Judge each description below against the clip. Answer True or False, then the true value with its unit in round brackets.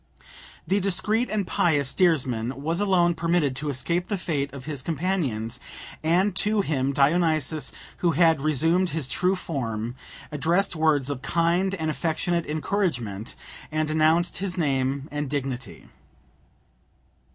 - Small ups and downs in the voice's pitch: False (4.3 semitones)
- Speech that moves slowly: True (130 wpm)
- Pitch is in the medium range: True (155 Hz)